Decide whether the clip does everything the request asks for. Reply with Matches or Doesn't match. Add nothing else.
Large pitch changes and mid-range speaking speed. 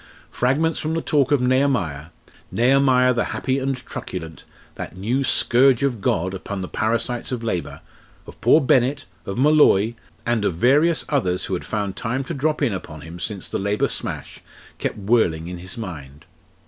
Matches